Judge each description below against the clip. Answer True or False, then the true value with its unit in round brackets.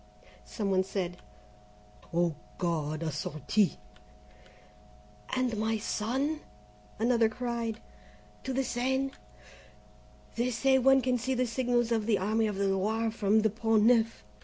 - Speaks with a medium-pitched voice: False (225 Hz)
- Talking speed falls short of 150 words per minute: True (135 wpm)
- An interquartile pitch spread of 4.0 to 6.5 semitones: False (3.6 semitones)